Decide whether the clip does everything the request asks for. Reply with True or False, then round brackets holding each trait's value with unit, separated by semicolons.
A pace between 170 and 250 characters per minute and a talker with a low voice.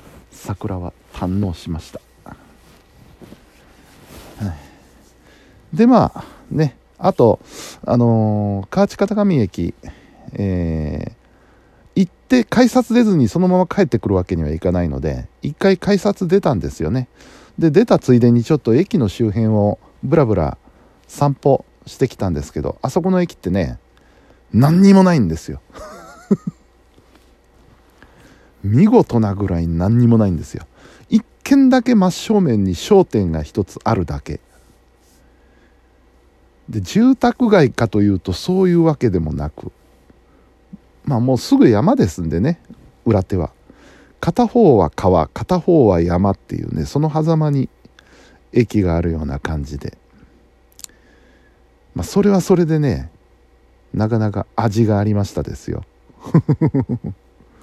True (235 characters per minute; 110 Hz)